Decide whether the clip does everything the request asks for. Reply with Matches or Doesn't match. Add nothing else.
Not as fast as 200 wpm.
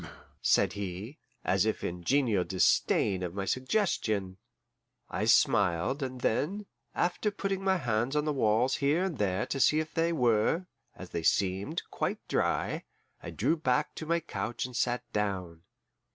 Matches